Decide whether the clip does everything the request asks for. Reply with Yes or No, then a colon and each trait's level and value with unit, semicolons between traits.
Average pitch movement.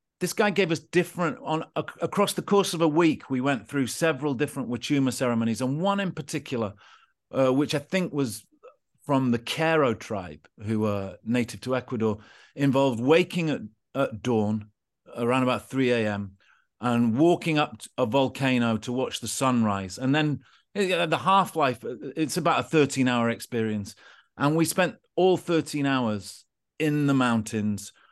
No: wide, 5.7 semitones